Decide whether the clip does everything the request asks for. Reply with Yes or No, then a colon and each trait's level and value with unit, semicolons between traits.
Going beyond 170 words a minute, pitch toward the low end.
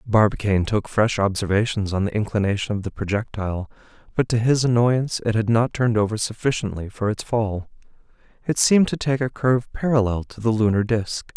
Yes: average, 180 wpm; low, 110 Hz